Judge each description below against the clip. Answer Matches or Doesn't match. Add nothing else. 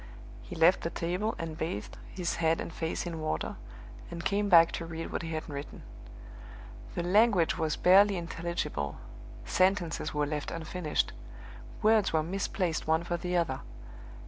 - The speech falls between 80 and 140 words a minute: Doesn't match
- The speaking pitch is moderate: Matches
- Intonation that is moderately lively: Doesn't match